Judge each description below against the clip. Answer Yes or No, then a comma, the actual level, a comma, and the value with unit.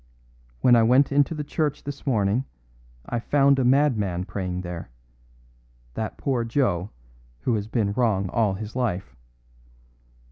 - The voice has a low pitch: Yes, low, 115 Hz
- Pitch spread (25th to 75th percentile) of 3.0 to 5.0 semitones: No, wide, 5.4 semitones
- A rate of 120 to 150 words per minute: Yes, average, 140 wpm